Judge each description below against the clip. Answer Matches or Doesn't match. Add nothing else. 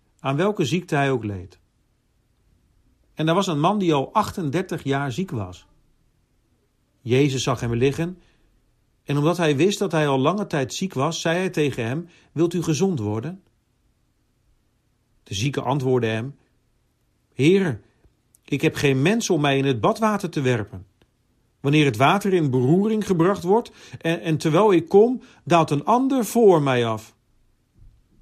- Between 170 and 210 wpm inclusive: Doesn't match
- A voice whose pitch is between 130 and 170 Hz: Matches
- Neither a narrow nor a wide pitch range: Doesn't match